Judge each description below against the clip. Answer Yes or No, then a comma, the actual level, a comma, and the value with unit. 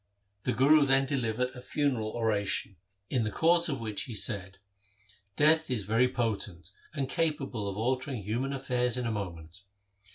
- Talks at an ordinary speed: Yes, average, 165 wpm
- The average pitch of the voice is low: Yes, low, 120 Hz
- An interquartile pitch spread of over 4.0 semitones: Yes, average, 4.6 semitones